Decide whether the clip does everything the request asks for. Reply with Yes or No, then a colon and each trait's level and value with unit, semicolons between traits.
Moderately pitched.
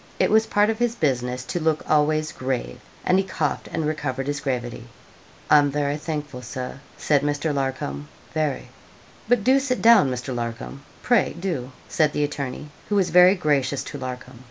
Yes: medium, 145 Hz